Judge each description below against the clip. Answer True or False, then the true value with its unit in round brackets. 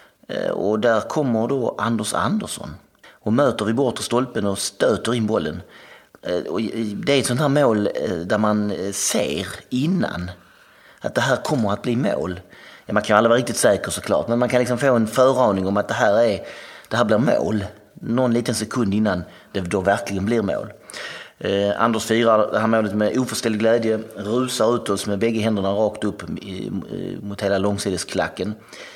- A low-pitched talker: True (110 Hz)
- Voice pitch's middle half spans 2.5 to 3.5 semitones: True (2.8 semitones)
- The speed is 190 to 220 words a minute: False (170 wpm)